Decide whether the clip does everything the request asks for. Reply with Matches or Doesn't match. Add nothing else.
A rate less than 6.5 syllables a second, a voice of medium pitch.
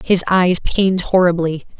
Matches